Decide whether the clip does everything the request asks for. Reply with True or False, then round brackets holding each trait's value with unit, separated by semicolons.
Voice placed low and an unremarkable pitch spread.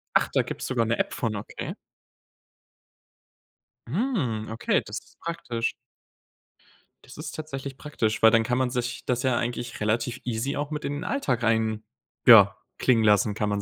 True (120 Hz; 3.5 semitones)